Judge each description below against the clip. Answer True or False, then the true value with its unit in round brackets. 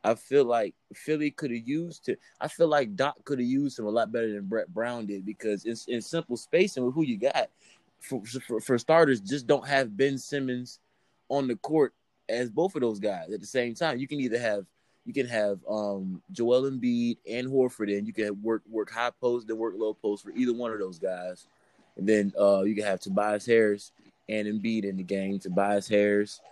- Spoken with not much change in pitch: False (3.9 semitones)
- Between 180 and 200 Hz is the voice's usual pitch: False (115 Hz)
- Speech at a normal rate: False (225 wpm)